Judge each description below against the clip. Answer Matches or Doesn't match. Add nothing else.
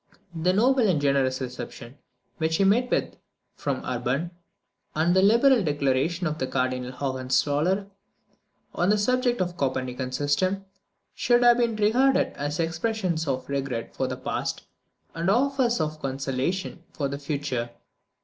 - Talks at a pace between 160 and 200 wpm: Doesn't match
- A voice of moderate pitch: Matches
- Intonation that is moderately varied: Doesn't match